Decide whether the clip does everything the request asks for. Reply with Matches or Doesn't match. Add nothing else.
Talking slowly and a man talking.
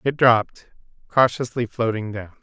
Matches